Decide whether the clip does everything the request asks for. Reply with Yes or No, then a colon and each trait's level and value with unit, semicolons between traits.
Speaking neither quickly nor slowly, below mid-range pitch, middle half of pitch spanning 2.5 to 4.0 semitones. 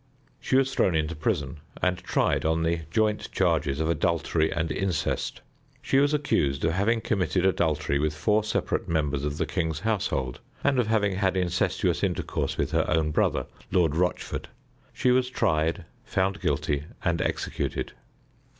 No: average, 160 wpm; very low, 85 Hz; average, 4.7 semitones